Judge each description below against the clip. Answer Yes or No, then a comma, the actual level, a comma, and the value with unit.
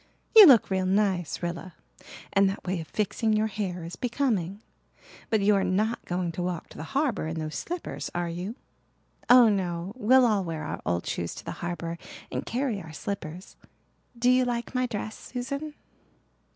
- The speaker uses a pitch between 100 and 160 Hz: No, high, 200 Hz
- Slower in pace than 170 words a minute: No, average, 180 wpm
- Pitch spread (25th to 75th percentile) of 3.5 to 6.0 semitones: Yes, wide, 5.4 semitones